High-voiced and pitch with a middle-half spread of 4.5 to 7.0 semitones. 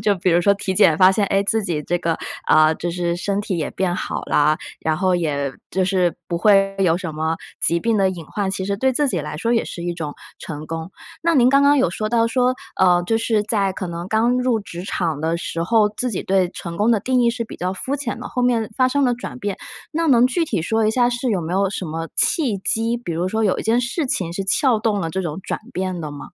Yes: high, 195 Hz; average, 5.2 semitones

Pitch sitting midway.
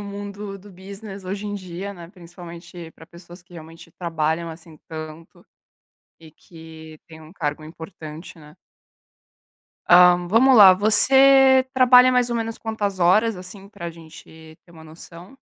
Yes: medium, 180 Hz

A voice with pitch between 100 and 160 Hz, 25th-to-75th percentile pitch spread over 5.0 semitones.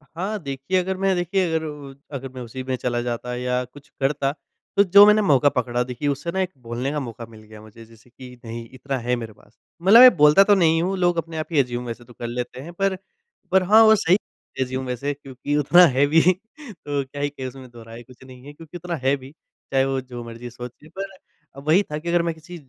Yes: medium, 140 Hz; wide, 5.6 semitones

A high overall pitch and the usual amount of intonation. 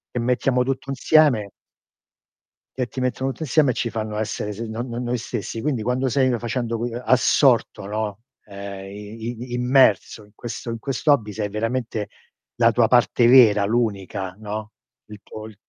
No: low, 115 Hz; average, 3.0 semitones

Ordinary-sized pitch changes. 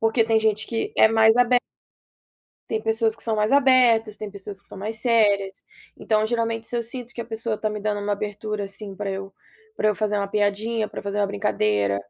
No: narrow, 1.8 semitones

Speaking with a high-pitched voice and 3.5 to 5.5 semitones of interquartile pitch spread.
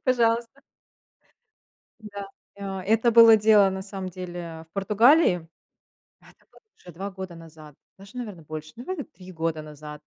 Yes: high, 195 Hz; average, 5.2 semitones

